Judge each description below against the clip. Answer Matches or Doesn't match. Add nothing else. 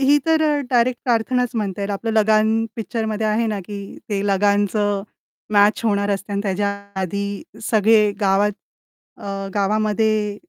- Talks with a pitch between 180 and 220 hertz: Matches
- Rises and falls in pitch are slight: Matches